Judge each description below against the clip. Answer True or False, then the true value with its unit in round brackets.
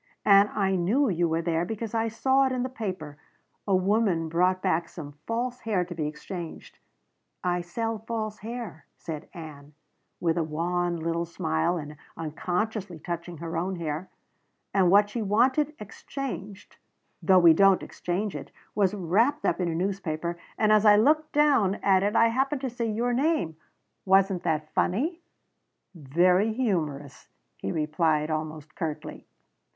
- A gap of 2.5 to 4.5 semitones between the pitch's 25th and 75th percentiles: False (5.2 semitones)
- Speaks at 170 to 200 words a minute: False (155 wpm)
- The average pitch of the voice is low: False (185 Hz)